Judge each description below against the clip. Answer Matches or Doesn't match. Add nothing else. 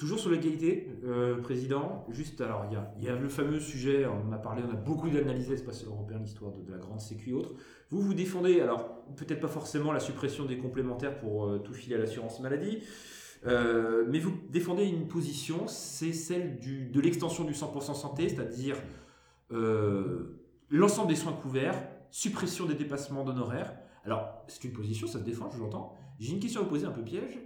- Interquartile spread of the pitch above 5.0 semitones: Matches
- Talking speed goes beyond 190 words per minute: Matches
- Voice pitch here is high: Doesn't match